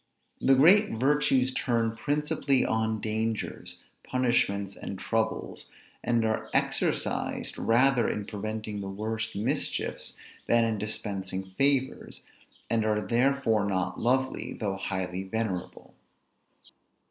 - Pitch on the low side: Yes, low, 110 Hz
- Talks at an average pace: No, slow, 110 wpm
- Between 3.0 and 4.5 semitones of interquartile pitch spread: Yes, average, 3.9 semitones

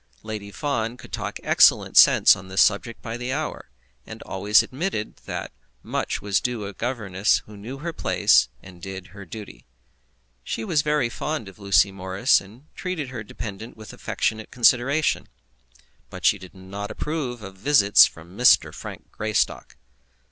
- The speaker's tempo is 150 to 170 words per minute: Yes, average, 160 wpm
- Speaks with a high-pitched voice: No, low, 110 Hz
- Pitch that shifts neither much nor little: Yes, average, 4.2 semitones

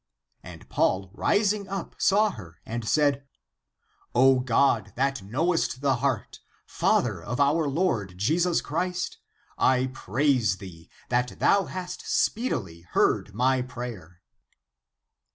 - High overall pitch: No, low, 130 Hz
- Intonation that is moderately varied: No, wide, 7.4 semitones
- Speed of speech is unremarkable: No, slow, 130 wpm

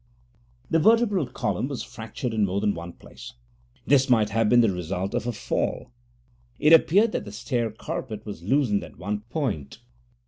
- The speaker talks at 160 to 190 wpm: Yes, average, 175 wpm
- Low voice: Yes, low, 115 Hz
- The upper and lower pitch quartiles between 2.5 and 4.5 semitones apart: No, average, 5.1 semitones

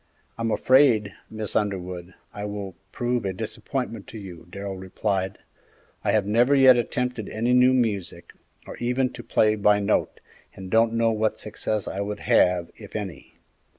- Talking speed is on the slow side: No, average, 160 wpm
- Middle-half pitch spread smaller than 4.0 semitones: Yes, average, 3.4 semitones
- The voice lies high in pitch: No, low, 105 Hz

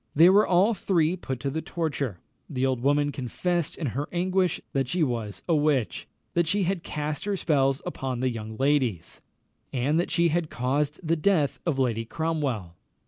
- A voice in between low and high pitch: Yes, medium, 145 Hz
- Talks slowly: No, average, 185 wpm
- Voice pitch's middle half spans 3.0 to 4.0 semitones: No, average, 4.7 semitones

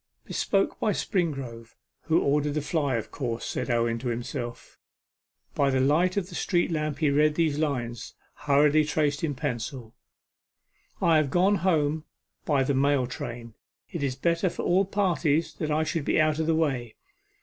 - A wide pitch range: No, average, 3.6 semitones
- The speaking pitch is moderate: Yes, medium, 150 Hz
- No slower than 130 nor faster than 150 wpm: No, average, 170 wpm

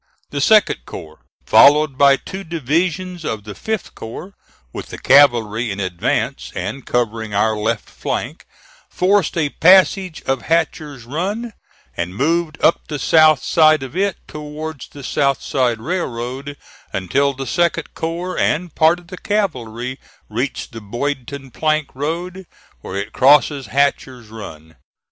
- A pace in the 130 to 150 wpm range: Yes, average, 140 wpm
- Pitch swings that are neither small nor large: No, wide, 6.0 semitones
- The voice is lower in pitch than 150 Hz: Yes, medium, 140 Hz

